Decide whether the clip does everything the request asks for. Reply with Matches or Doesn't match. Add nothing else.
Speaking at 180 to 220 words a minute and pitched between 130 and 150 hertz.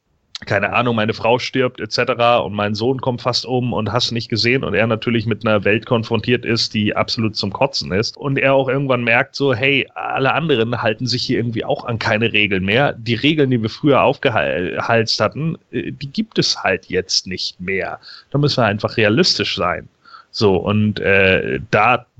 Doesn't match